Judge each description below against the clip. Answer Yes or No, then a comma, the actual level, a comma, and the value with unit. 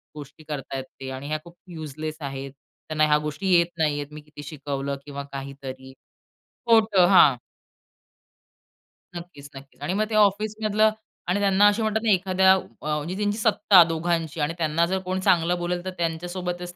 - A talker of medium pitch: Yes, medium, 170 Hz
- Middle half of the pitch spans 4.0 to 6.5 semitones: Yes, average, 4.4 semitones